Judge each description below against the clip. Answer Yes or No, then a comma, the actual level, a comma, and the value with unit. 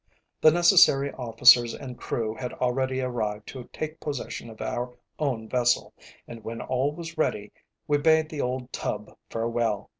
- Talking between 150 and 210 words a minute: Yes, average, 155 wpm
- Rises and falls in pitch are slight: No, average, 3.7 semitones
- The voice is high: No, low, 125 Hz